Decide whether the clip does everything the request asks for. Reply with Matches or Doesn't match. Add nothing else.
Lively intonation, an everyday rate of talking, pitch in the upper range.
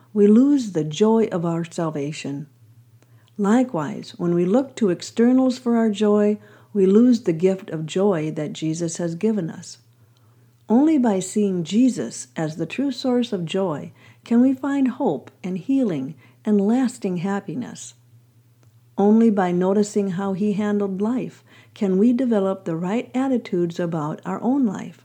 Matches